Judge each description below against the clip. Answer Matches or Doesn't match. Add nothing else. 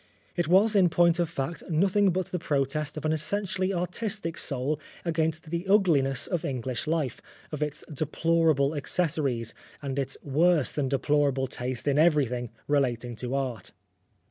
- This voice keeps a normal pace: Matches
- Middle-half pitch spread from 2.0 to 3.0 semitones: Doesn't match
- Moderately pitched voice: Matches